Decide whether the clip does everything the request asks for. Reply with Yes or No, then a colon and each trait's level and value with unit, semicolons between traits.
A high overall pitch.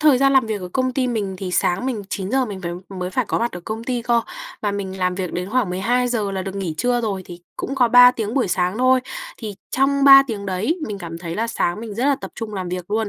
Yes: high, 215 Hz